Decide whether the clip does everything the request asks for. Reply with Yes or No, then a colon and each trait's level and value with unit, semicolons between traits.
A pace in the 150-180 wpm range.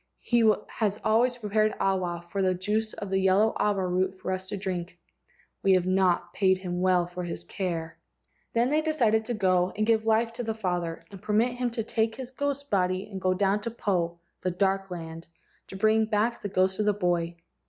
No: fast, 205 wpm